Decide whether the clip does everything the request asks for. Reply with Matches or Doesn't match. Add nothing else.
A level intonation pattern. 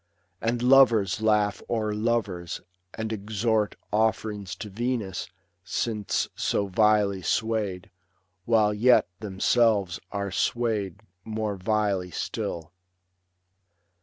Matches